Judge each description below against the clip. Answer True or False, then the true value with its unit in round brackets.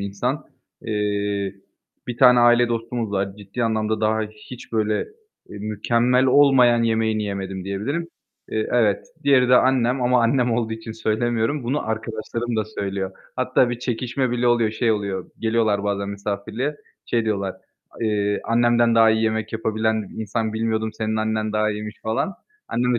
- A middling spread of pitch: False (2.1 semitones)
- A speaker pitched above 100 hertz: True (110 Hz)